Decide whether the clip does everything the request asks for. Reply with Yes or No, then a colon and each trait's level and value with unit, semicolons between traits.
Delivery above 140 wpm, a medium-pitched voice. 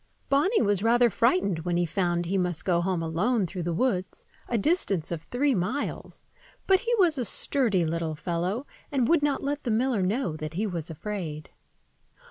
No: average, 185 wpm; high, 195 Hz